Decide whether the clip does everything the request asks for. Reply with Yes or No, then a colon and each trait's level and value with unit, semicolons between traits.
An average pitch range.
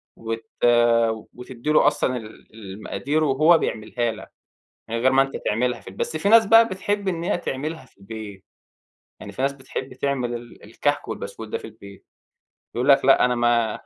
Yes: average, 4.6 semitones